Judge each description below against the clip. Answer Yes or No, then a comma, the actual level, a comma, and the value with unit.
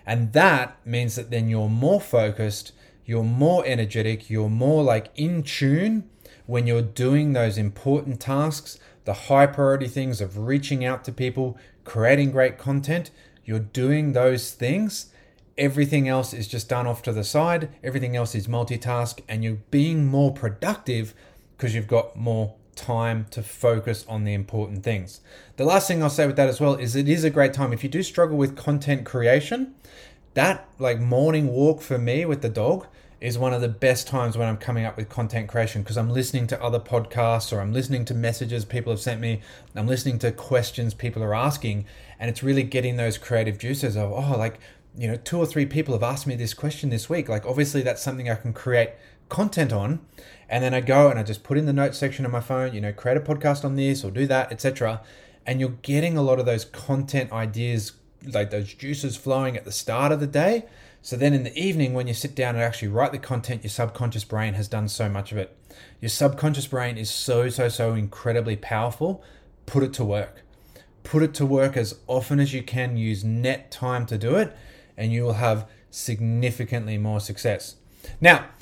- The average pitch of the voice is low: Yes, low, 125 Hz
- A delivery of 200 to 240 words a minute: Yes, fast, 205 wpm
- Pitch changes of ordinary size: Yes, average, 3.5 semitones